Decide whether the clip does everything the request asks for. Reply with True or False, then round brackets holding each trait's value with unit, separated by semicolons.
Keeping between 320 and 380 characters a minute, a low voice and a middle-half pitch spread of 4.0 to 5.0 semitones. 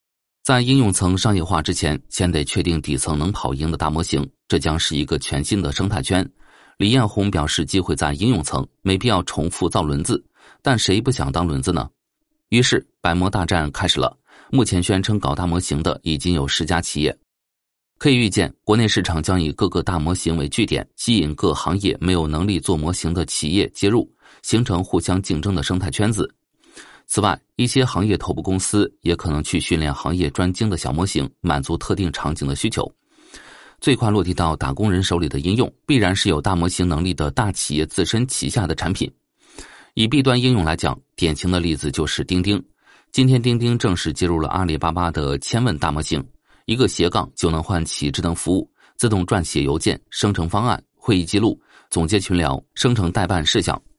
False (300 characters per minute; 90 Hz; 4.5 semitones)